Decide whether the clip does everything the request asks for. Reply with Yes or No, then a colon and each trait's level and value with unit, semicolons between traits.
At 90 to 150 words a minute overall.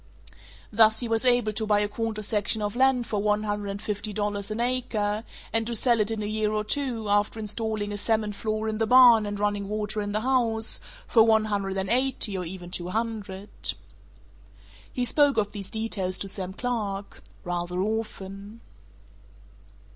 No: average, 185 wpm